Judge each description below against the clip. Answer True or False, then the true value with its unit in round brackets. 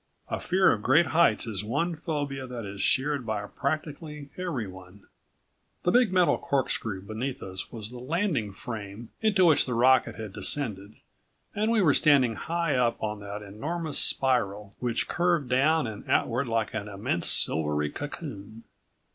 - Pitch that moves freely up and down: True (6.7 semitones)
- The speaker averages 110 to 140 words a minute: False (155 wpm)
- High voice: False (125 Hz)